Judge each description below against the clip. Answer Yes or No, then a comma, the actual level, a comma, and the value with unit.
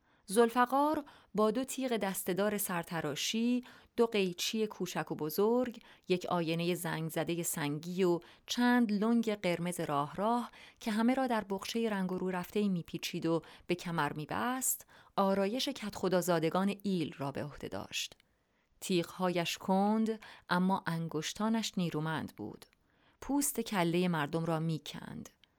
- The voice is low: No, medium, 185 Hz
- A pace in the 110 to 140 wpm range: Yes, slow, 135 wpm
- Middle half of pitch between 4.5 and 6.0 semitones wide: Yes, average, 4.9 semitones